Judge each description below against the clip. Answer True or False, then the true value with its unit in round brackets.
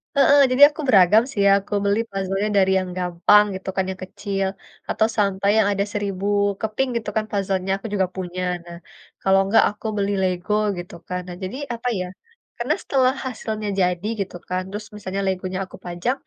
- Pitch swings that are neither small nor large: False (2.3 semitones)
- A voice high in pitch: True (200 Hz)